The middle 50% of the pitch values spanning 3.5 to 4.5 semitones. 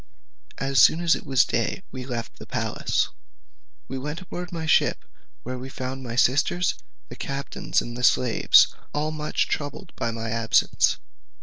Yes: average, 3.8 semitones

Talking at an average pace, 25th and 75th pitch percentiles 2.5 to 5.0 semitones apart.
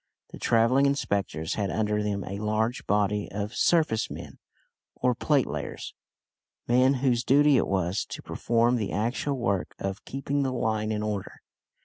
Yes: average, 155 wpm; average, 3.9 semitones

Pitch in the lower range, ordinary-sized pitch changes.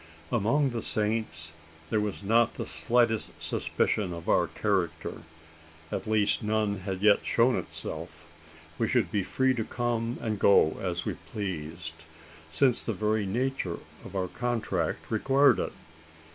Yes: low, 105 Hz; average, 3.9 semitones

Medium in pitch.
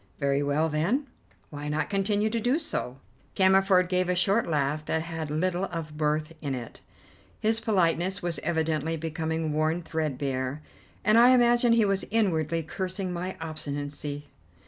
Yes: medium, 165 Hz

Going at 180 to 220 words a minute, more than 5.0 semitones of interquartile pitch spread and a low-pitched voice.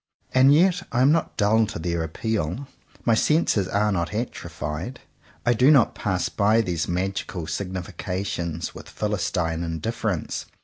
No: average, 140 wpm; wide, 5.6 semitones; low, 100 Hz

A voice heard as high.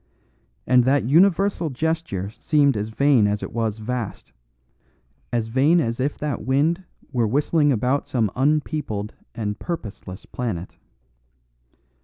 No: low, 130 Hz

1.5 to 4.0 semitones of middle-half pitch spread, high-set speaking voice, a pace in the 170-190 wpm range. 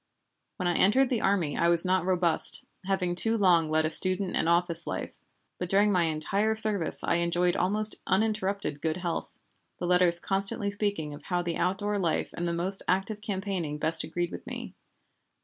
No: average, 2.9 semitones; medium, 180 Hz; average, 185 wpm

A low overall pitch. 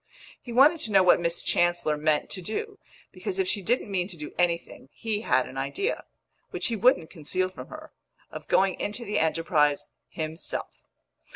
No: medium, 185 Hz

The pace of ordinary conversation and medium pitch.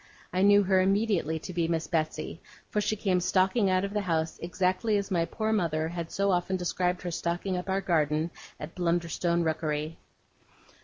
Yes: average, 185 wpm; medium, 180 Hz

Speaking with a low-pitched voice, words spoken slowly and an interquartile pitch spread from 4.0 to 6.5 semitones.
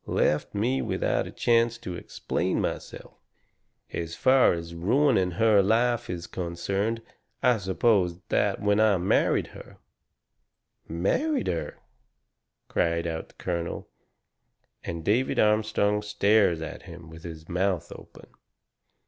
Yes: very low, 95 Hz; slow, 125 wpm; average, 4.7 semitones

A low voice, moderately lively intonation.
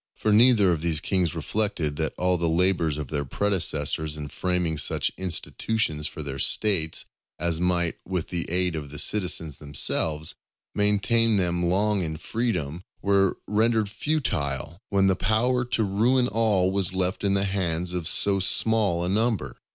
Yes: very low, 90 Hz; average, 4.3 semitones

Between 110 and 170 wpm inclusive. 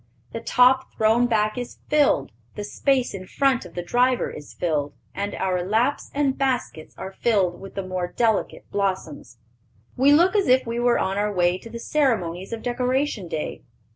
No: average, 180 wpm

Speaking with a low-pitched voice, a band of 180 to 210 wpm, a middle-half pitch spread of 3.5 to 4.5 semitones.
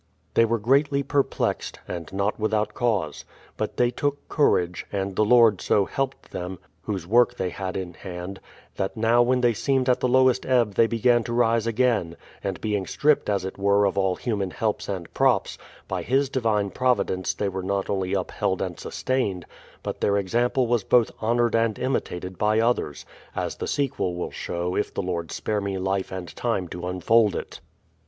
Yes: low, 105 Hz; average, 190 wpm; average, 4.2 semitones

